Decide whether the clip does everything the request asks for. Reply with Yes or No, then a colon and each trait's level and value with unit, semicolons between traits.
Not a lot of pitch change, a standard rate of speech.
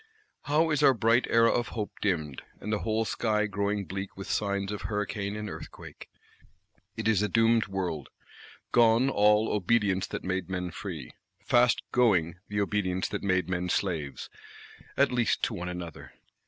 No: average, 3.3 semitones; average, 160 wpm